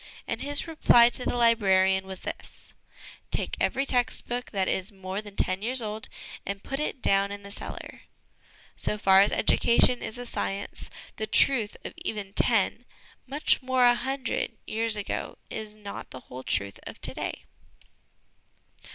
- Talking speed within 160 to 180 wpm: Yes, average, 170 wpm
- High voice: Yes, high, 215 Hz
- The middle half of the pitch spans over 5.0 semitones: No, average, 3.9 semitones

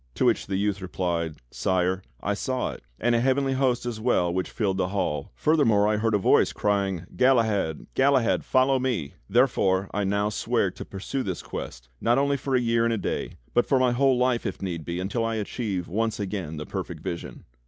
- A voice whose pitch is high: No, low, 105 Hz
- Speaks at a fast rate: Yes, fast, 215 wpm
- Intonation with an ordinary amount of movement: Yes, average, 4.9 semitones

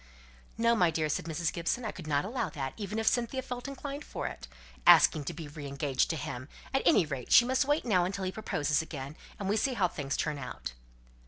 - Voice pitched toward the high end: No, medium, 175 Hz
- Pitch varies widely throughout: Yes, wide, 8.0 semitones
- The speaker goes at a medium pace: No, fast, 230 wpm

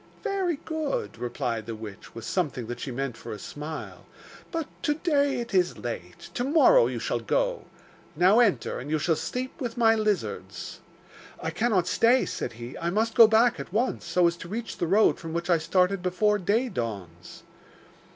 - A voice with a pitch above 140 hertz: Yes, medium, 185 Hz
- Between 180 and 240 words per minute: Yes, average, 190 wpm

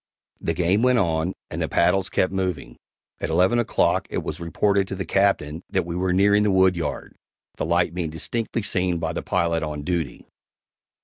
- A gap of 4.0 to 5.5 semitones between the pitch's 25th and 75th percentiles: No, average, 2.8 semitones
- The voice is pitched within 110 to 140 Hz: No, very low, 90 Hz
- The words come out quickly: No, average, 185 wpm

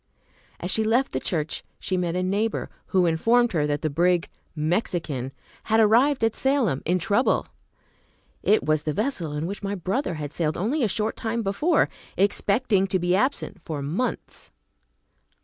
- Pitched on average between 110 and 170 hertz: No, high, 190 Hz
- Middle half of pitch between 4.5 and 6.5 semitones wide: Yes, wide, 5.5 semitones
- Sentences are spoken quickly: No, average, 165 wpm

